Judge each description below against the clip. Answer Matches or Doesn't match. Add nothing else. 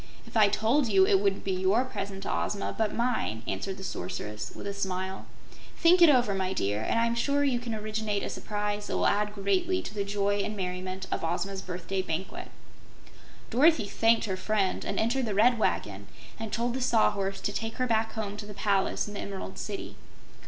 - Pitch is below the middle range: Doesn't match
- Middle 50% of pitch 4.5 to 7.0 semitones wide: Doesn't match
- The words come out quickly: Matches